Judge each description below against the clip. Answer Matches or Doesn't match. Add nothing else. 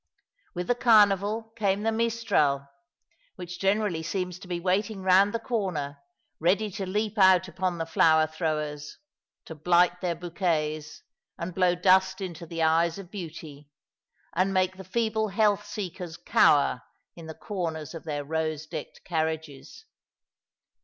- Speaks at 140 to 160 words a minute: Matches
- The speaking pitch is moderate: Matches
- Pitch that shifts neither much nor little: Matches